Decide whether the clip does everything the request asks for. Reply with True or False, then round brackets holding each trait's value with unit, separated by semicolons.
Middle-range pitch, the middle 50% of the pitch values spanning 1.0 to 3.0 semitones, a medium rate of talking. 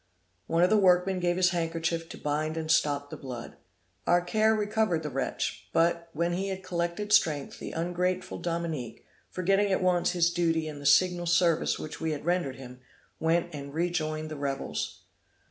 True (170 Hz; 2.6 semitones; 180 wpm)